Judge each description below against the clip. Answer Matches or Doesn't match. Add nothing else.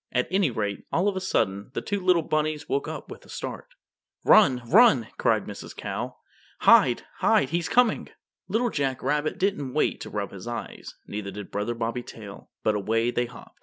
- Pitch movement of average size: Doesn't match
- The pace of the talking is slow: Doesn't match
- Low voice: Matches